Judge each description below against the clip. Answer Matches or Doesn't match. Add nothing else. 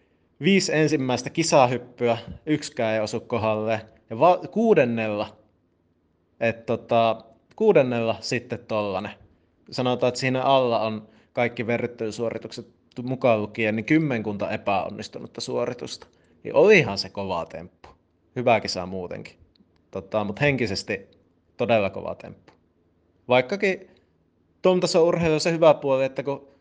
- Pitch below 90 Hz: Doesn't match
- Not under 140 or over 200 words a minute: Doesn't match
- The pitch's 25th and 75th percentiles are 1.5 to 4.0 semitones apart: Doesn't match